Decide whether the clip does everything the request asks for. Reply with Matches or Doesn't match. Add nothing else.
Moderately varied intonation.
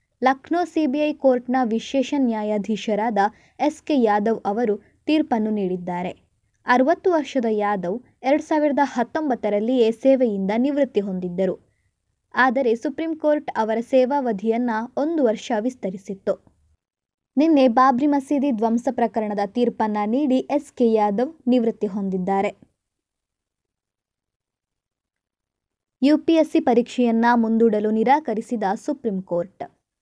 Matches